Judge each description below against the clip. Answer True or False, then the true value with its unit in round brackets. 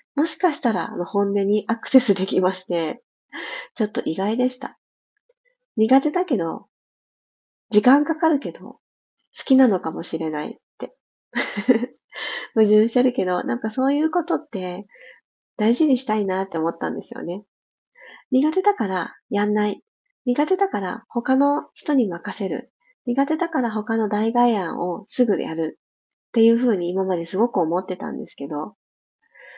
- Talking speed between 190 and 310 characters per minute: True (290 characters per minute)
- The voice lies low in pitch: False (230 Hz)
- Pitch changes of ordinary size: False (6.1 semitones)